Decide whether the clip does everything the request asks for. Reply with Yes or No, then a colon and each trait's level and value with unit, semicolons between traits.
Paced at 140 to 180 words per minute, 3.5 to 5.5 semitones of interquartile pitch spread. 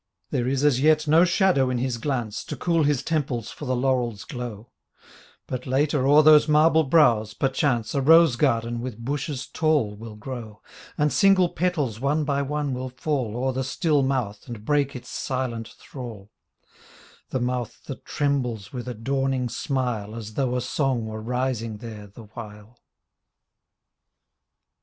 Yes: average, 160 wpm; average, 3.9 semitones